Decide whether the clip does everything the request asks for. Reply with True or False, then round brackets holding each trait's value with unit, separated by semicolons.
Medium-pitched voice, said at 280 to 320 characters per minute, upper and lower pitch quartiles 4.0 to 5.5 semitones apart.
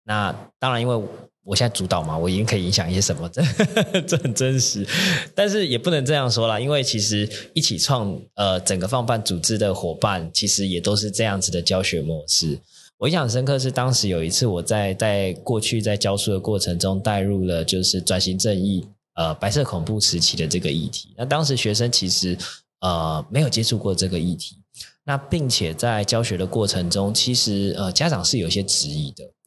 False (100 Hz; 300 characters per minute; 4.7 semitones)